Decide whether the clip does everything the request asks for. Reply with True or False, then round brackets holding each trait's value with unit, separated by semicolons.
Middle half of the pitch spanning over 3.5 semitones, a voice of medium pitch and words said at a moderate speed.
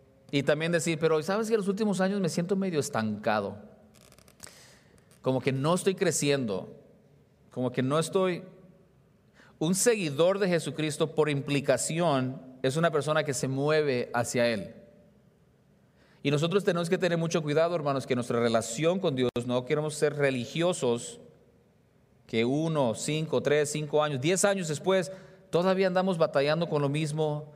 True (4.2 semitones; 155 Hz; 150 wpm)